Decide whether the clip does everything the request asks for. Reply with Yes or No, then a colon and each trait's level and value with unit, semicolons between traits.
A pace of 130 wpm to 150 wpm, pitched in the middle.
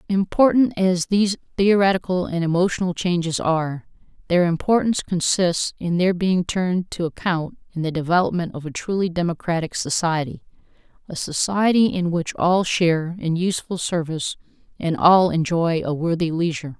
Yes: average, 145 wpm; medium, 175 Hz